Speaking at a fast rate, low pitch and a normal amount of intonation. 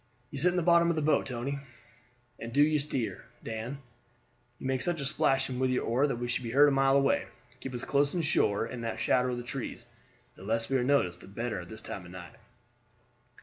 Yes: fast, 235 wpm; low, 130 Hz; average, 3.5 semitones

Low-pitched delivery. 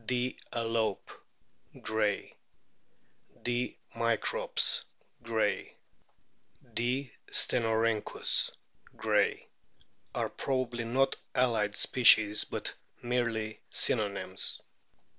Yes: low, 115 Hz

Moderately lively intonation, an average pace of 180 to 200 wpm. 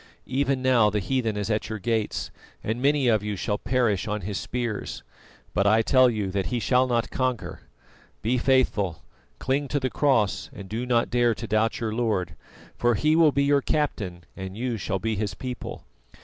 Yes: average, 3.7 semitones; average, 190 wpm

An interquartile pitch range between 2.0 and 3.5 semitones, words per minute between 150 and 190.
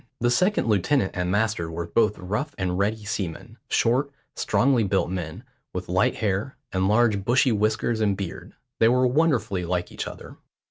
No: average, 4.2 semitones; average, 170 wpm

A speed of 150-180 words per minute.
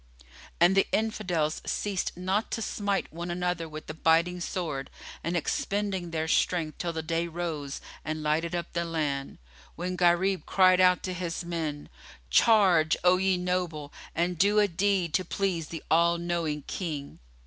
Yes: average, 160 wpm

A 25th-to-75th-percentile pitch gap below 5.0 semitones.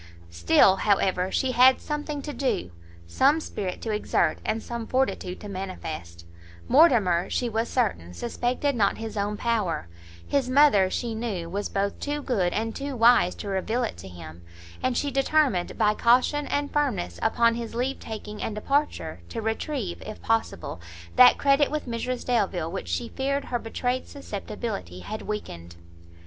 No: wide, 5.5 semitones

